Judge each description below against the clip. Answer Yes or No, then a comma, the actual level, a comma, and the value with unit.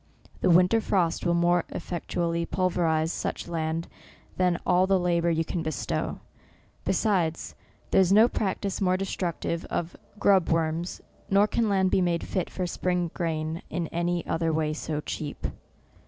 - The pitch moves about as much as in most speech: No, narrow, 2.1 semitones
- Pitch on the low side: No, medium, 175 Hz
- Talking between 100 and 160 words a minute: Yes, average, 155 wpm